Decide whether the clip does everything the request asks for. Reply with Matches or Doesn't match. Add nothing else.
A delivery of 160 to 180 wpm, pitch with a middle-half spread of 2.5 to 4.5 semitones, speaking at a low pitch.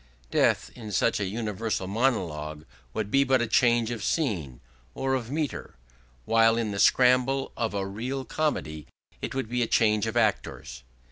Matches